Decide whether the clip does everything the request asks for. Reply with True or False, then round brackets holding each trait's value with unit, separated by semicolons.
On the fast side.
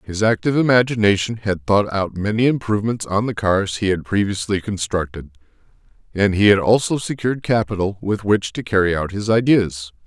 False (165 wpm)